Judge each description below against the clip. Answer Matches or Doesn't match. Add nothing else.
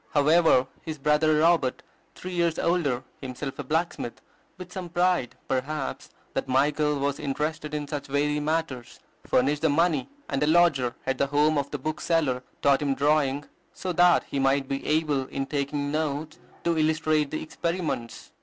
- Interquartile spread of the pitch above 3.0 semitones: Doesn't match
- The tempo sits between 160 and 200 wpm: Matches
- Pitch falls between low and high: Matches